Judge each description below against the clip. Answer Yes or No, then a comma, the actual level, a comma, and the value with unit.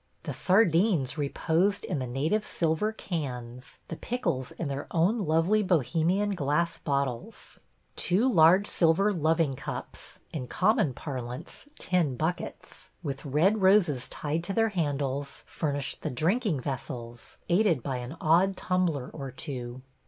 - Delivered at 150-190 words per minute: No, slow, 135 wpm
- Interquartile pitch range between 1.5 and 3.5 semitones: No, wide, 5.5 semitones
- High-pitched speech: No, medium, 160 Hz